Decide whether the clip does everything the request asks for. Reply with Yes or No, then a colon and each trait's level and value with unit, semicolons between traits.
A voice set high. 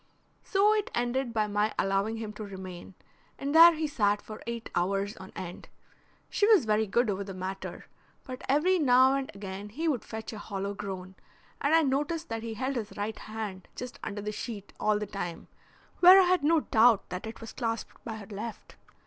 Yes: high, 220 Hz